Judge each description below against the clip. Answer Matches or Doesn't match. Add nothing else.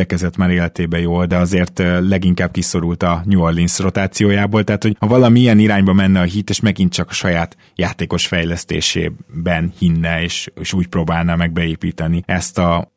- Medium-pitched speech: Doesn't match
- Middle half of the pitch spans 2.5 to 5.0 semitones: Doesn't match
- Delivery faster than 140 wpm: Matches